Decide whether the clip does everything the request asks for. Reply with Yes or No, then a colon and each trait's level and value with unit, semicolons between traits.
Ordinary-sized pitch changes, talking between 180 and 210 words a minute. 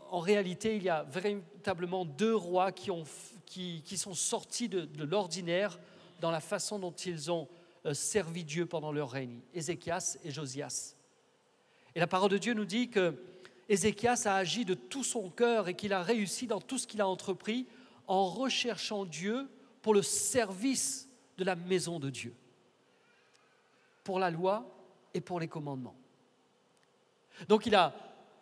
No: average, 3.7 semitones; average, 165 wpm